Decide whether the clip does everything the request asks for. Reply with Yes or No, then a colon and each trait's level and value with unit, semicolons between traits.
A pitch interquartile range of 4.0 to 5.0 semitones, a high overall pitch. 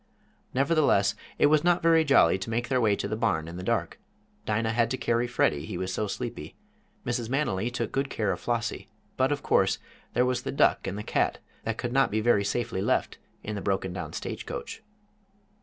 No: average, 4.5 semitones; low, 115 Hz